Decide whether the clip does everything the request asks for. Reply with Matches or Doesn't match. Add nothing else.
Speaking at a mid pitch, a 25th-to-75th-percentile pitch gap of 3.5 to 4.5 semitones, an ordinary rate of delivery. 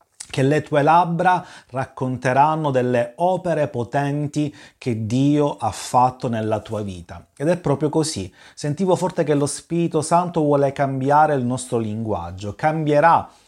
Matches